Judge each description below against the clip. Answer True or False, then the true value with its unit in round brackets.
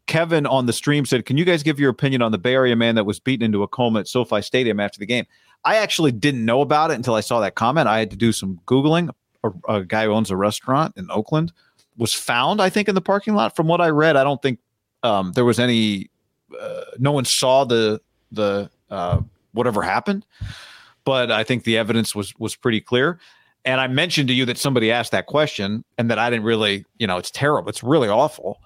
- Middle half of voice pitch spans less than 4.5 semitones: False (5.0 semitones)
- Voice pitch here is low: True (125 Hz)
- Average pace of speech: False (235 wpm)